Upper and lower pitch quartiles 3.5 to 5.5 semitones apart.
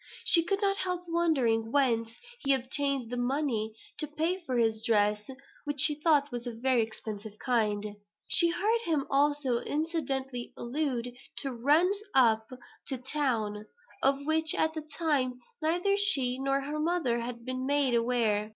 Yes: average, 4.6 semitones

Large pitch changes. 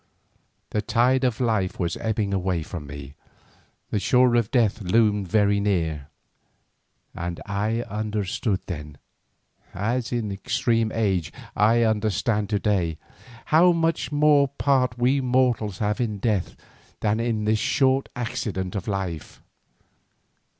No: average, 3.8 semitones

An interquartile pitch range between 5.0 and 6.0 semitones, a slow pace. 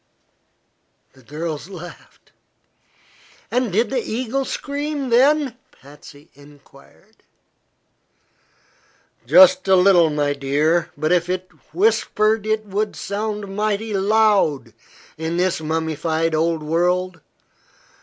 Yes: wide, 5.4 semitones; slow, 100 wpm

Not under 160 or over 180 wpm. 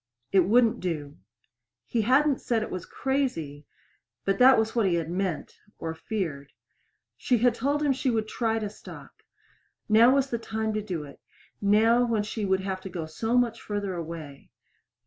Yes: average, 175 wpm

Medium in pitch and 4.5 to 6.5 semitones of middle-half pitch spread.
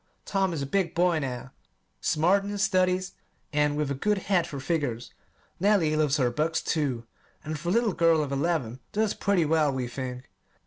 Yes: medium, 155 Hz; average, 4.9 semitones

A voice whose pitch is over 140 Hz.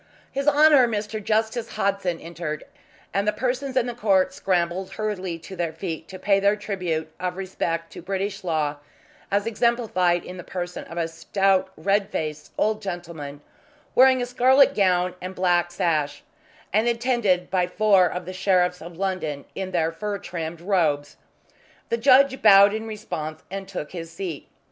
Yes: high, 190 Hz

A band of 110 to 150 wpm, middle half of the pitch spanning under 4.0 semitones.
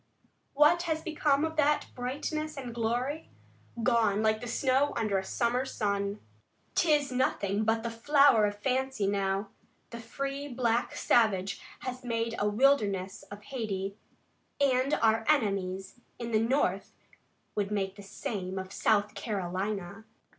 No: slow, 135 wpm; average, 4.9 semitones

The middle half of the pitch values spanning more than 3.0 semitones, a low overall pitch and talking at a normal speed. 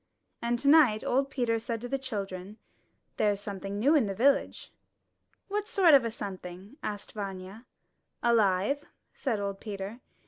No: average, 4.8 semitones; high, 220 Hz; average, 145 wpm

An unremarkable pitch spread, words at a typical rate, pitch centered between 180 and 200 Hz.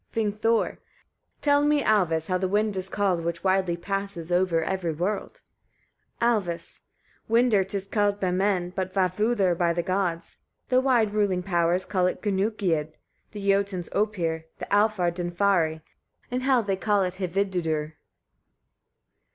Yes: average, 3.0 semitones; average, 150 wpm; high, 190 Hz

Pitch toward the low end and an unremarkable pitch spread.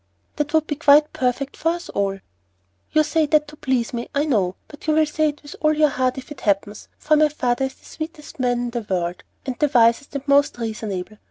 No: very high, 275 Hz; average, 4.4 semitones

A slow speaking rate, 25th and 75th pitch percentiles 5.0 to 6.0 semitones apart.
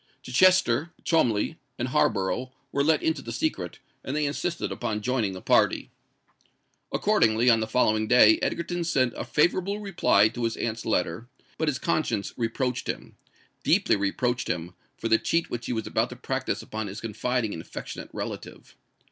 No: average, 165 wpm; wide, 5.6 semitones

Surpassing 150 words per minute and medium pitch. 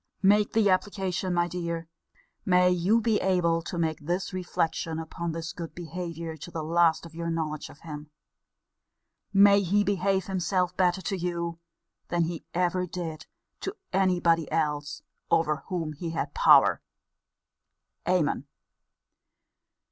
No: average, 140 wpm; medium, 175 Hz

